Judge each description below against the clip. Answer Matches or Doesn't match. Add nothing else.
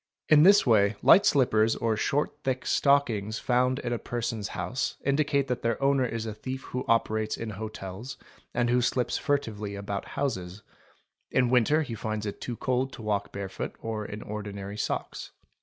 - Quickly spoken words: Doesn't match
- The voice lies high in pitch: Doesn't match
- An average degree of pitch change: Matches